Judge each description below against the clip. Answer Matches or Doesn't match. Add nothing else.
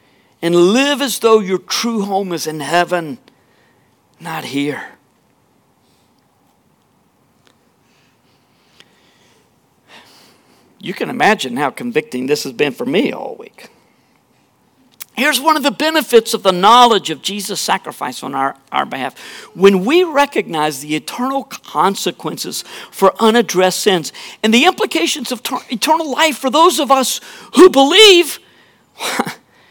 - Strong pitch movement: Matches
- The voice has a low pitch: Doesn't match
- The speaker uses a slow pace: Matches